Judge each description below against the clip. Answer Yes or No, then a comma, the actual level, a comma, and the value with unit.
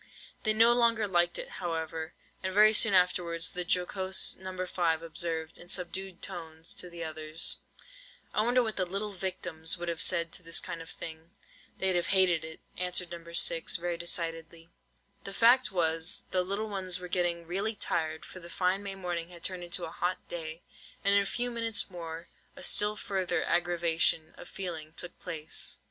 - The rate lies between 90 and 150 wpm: No, average, 185 wpm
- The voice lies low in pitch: No, medium, 175 Hz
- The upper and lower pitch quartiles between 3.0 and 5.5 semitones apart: No, narrow, 2.4 semitones